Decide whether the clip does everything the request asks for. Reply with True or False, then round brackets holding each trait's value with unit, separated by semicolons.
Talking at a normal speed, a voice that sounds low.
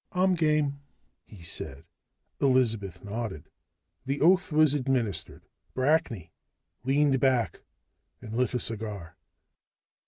False (100 wpm; 130 Hz)